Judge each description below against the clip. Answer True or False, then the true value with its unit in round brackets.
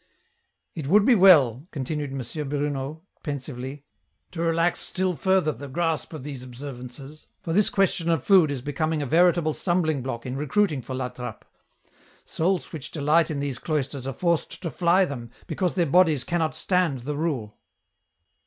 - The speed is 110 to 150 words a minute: False (170 wpm)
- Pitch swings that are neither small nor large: True (4.1 semitones)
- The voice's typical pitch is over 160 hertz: False (150 Hz)